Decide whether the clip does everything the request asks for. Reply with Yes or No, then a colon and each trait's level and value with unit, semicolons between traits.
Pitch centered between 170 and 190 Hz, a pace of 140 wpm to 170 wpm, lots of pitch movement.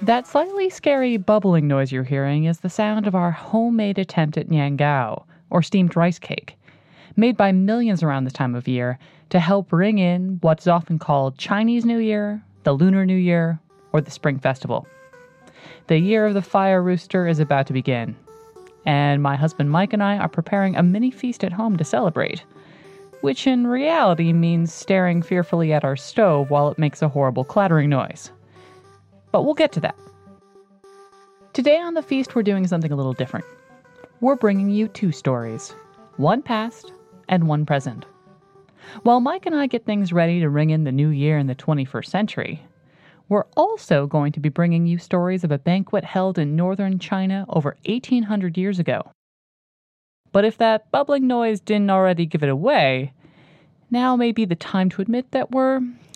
No: medium, 185 Hz; average, 180 wpm; wide, 5.8 semitones